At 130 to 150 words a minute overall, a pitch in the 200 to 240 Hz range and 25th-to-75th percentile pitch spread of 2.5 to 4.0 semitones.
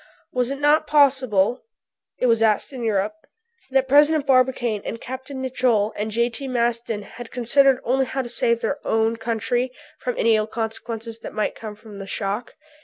No: average, 175 wpm; high, 235 Hz; average, 2.9 semitones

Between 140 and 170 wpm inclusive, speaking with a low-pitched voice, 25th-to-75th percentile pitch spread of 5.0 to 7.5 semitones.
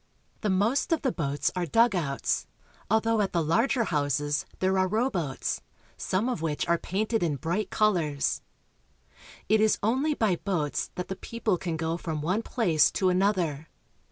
No: average, 160 wpm; medium, 185 Hz; average, 5.3 semitones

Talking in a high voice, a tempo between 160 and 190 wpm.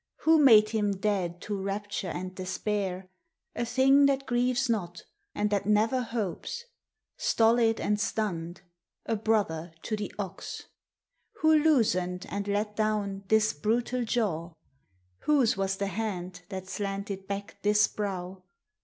No: high, 205 Hz; slow, 135 wpm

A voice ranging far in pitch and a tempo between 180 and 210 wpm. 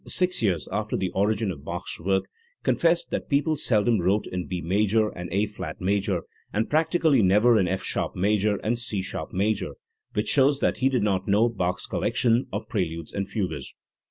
No: average, 4.0 semitones; average, 185 wpm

